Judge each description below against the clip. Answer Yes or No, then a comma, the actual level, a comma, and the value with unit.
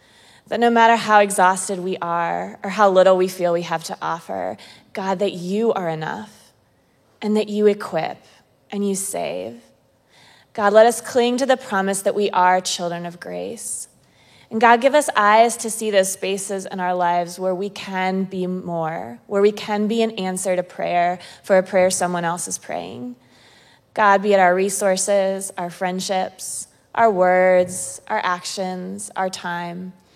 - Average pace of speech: Yes, average, 170 wpm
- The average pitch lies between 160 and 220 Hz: Yes, high, 190 Hz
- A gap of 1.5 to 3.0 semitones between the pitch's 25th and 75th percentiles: Yes, narrow, 2.5 semitones